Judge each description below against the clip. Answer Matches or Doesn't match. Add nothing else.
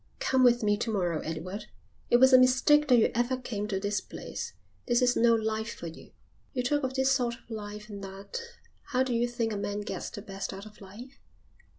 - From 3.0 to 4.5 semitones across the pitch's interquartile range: Matches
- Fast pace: Matches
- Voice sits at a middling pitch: Doesn't match